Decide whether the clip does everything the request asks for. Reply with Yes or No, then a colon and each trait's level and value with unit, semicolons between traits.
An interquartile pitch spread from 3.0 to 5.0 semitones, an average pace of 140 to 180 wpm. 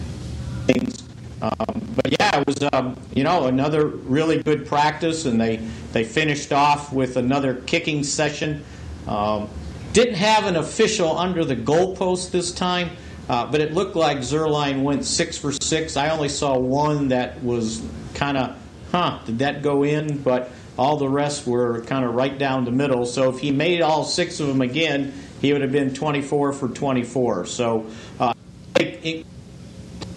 Yes: average, 3.7 semitones; average, 170 wpm